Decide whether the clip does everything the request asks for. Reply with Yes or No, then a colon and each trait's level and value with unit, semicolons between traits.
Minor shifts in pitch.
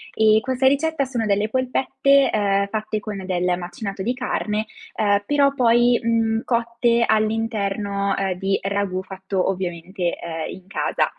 No: average, 3.4 semitones